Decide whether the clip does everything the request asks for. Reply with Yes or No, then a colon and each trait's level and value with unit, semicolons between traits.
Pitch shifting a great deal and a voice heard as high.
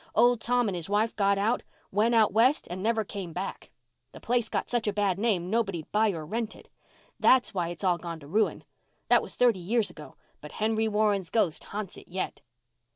No: average, 3.6 semitones; high, 210 Hz